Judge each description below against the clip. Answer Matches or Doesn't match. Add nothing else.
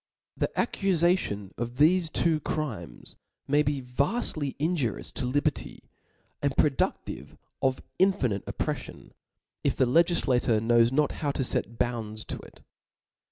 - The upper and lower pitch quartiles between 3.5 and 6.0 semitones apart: Matches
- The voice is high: Doesn't match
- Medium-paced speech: Doesn't match